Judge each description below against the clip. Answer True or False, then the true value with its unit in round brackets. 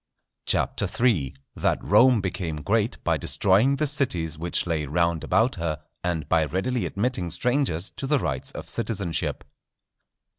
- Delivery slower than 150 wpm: True (140 wpm)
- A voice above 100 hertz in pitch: False (90 Hz)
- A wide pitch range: True (7.3 semitones)